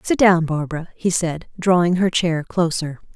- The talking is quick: No, average, 170 wpm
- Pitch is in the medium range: Yes, medium, 170 Hz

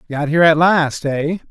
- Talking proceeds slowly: No, average, 200 wpm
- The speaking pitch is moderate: Yes, medium, 155 Hz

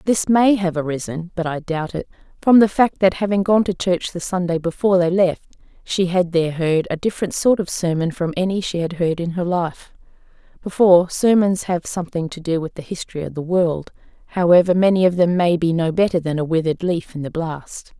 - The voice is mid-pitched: Yes, medium, 175 Hz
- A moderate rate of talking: No, fast, 210 wpm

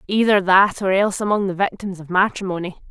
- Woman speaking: Yes, female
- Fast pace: No, average, 185 wpm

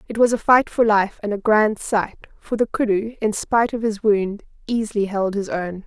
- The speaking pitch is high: Yes, high, 215 Hz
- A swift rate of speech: Yes, fast, 225 wpm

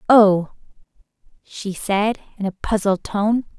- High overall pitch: Yes, high, 205 Hz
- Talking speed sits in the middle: No, slow, 115 wpm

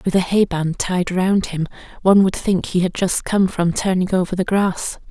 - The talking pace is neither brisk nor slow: No, fast, 225 wpm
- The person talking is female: Yes, female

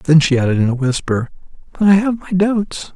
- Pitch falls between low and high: Yes, medium, 165 Hz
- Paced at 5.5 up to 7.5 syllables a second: No, 5.3 syllables/s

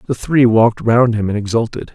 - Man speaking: Yes, male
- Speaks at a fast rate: Yes, fast, 215 wpm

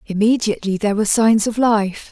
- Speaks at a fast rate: No, average, 170 wpm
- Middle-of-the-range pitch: No, high, 215 Hz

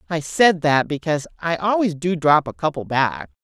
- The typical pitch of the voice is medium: Yes, medium, 160 Hz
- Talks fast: No, average, 190 wpm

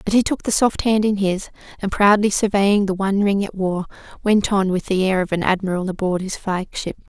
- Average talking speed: No, fast, 225 wpm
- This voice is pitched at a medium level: No, high, 195 Hz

